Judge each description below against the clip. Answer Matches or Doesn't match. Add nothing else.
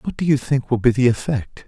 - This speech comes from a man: Matches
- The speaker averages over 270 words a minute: Matches